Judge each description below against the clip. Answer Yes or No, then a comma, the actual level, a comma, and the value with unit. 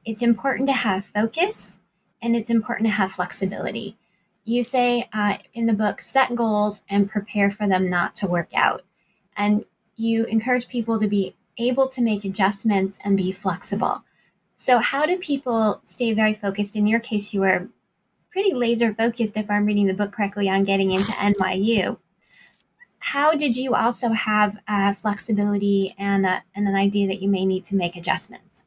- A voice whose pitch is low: No, high, 210 Hz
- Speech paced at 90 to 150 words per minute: No, average, 175 wpm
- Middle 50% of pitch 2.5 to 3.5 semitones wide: Yes, average, 3.1 semitones